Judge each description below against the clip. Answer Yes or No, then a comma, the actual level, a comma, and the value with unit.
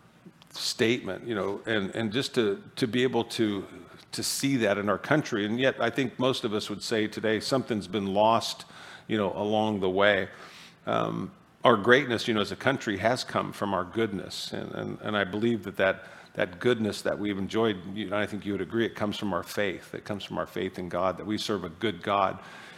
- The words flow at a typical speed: No, fast, 225 wpm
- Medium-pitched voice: No, low, 105 Hz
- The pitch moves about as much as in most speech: No, narrow, 2.3 semitones